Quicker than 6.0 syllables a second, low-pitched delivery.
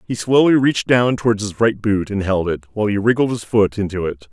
No: 5.9 syllables/s; low, 105 Hz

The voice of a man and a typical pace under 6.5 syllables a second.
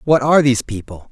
No: male; 7.1 syllables/s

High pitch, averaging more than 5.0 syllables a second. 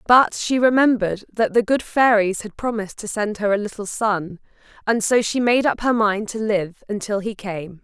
No: high, 215 Hz; 4.9 syllables/s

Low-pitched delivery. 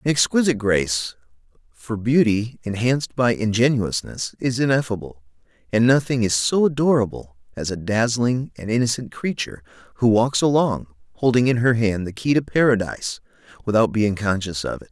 Yes: low, 115 Hz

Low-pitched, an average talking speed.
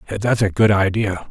Yes: low, 100 Hz; average, 185 wpm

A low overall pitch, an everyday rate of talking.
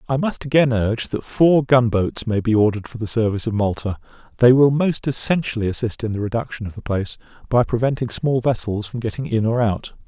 No: low, 115 Hz; fast, 215 wpm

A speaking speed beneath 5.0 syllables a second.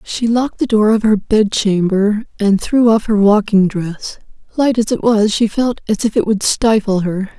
Yes: 4.6 syllables/s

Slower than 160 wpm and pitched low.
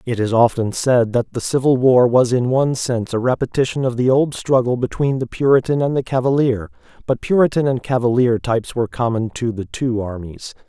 No: average, 195 wpm; low, 125 Hz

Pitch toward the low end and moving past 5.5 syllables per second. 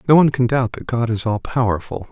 Yes: low, 120 Hz; 6.2 syllables/s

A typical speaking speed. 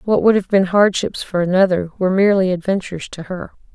Yes: average, 190 wpm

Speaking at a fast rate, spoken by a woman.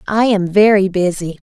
No: average, 165 wpm; female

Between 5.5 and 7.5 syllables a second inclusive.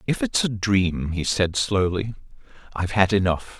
No: 4.6 syllables/s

